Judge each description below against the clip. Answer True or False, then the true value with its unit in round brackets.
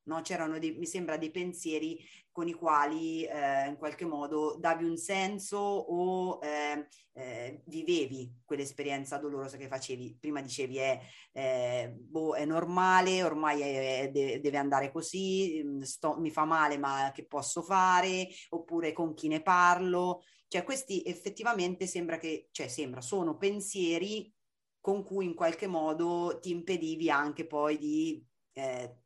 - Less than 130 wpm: False (145 wpm)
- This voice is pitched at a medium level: True (160 Hz)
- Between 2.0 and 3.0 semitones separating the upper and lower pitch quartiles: False (3.8 semitones)